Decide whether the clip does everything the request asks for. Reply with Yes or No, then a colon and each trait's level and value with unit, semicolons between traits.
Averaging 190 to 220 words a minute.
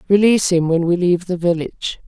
Yes: average, 200 wpm